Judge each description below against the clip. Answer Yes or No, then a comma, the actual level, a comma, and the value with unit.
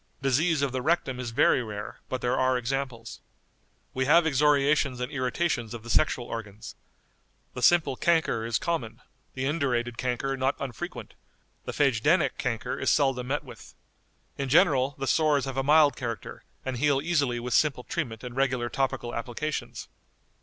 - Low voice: Yes, low, 130 Hz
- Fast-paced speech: No, average, 160 wpm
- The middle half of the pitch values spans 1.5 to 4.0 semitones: Yes, average, 3.1 semitones